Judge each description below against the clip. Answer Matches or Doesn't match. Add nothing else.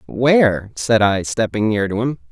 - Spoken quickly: Doesn't match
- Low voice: Matches